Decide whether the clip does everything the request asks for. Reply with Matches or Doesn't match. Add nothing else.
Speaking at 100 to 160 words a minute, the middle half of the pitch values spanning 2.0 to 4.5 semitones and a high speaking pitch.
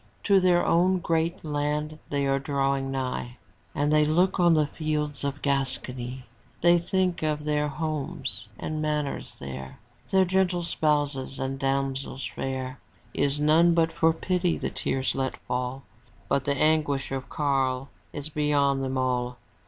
Doesn't match